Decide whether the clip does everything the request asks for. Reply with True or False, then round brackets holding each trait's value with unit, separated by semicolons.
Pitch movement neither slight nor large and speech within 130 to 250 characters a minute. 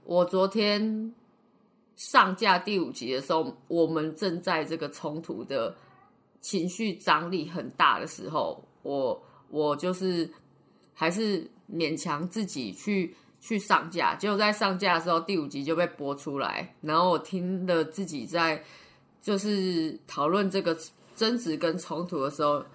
True (4.2 semitones; 210 characters per minute)